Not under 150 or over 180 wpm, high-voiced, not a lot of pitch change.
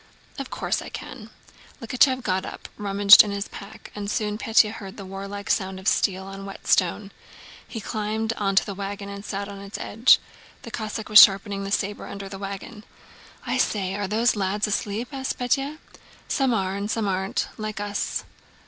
Yes: average, 175 wpm; high, 205 Hz; narrow, 1.7 semitones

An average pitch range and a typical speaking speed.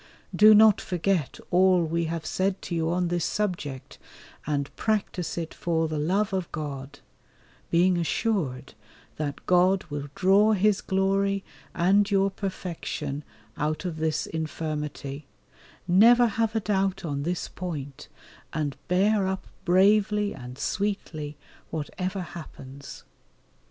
No: average, 4.2 semitones; slow, 125 wpm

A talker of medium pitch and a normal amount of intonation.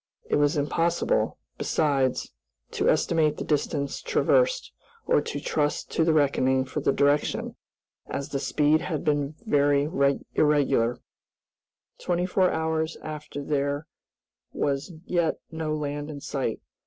No: medium, 150 Hz; narrow, 2.1 semitones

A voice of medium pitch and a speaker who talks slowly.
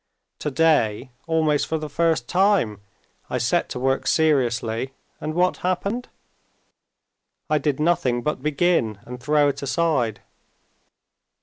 Yes: medium, 150 Hz; slow, 120 wpm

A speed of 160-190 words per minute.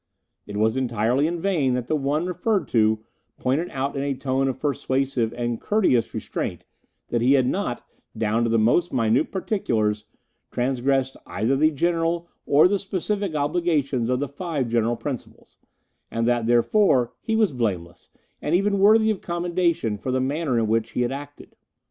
Yes: average, 170 wpm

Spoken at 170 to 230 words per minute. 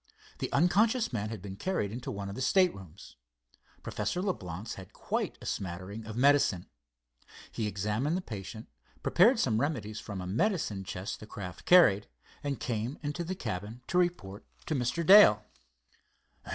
No: average, 155 wpm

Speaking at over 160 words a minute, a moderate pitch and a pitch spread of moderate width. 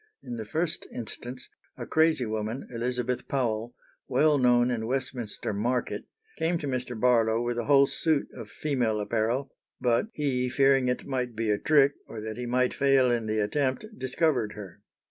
No: average, 170 wpm; low, 125 Hz; average, 3.1 semitones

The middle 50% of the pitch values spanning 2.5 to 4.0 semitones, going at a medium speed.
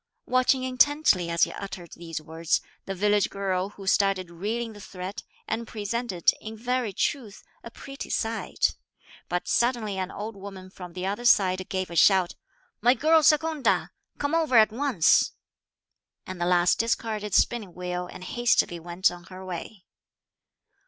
No: average, 4.5 semitones; average, 160 wpm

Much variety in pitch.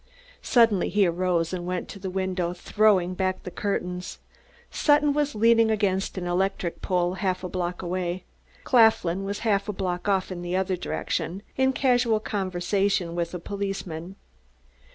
No: narrow, 2.6 semitones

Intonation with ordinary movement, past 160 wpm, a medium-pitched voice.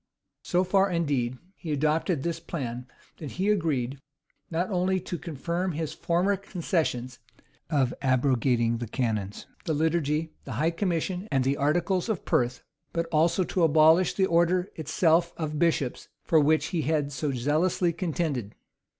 No: average, 4.2 semitones; average, 150 wpm; medium, 160 Hz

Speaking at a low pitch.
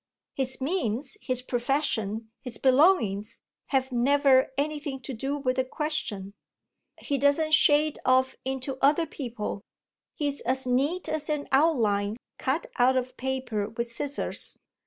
No: very high, 265 Hz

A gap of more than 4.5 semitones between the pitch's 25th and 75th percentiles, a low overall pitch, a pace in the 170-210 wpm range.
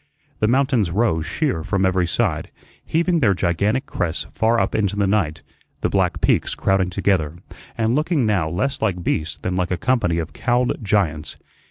Yes: wide, 5.4 semitones; low, 100 Hz; average, 175 wpm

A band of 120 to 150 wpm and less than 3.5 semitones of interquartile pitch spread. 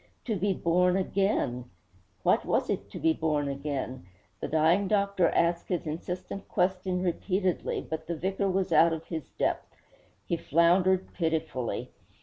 Yes: average, 145 wpm; average, 2.9 semitones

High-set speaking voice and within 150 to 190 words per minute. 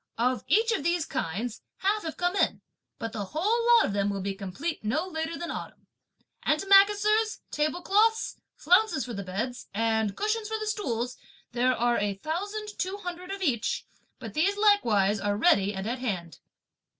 Yes: very high, 310 Hz; average, 175 wpm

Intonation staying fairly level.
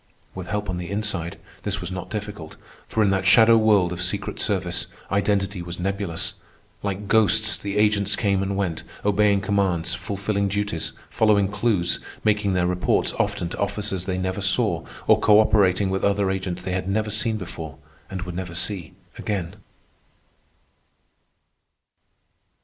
Yes: narrow, 2.2 semitones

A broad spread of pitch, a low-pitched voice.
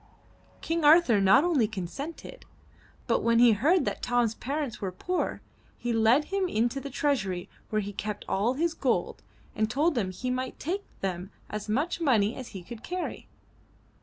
No: wide, 6.1 semitones; high, 245 Hz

